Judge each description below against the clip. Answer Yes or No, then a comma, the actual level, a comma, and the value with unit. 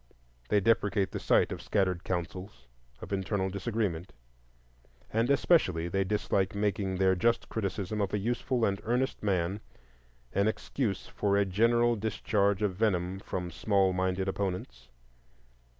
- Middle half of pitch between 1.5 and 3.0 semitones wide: Yes, narrow, 2.5 semitones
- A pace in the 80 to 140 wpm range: Yes, slow, 135 wpm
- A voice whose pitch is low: Yes, low, 100 Hz